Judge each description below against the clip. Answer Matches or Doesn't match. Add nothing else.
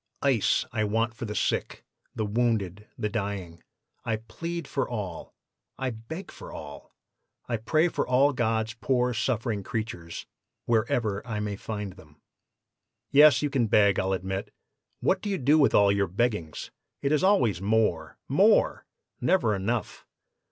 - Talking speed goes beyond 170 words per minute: Doesn't match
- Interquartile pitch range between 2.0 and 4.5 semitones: Matches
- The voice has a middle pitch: Doesn't match